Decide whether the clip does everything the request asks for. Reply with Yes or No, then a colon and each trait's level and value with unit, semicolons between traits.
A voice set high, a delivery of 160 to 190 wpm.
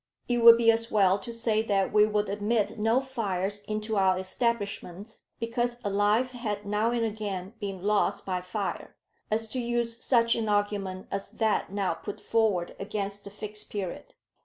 Yes: high, 210 Hz; average, 175 wpm